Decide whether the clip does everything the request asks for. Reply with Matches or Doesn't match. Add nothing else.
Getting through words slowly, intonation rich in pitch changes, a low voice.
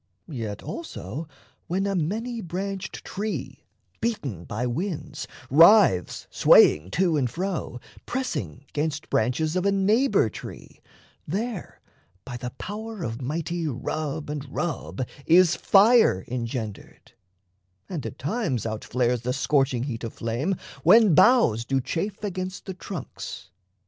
Doesn't match